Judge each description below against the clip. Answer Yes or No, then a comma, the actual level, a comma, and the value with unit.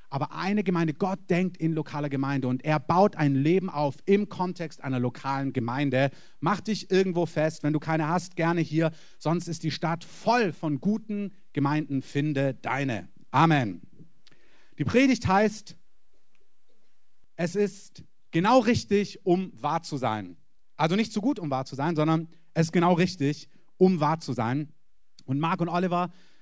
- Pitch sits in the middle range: Yes, medium, 165 Hz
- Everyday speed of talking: Yes, average, 165 wpm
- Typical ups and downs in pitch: Yes, average, 4.3 semitones